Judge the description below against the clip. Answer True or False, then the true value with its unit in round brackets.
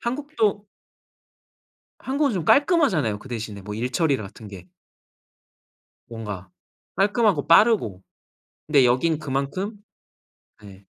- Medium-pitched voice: True (145 Hz)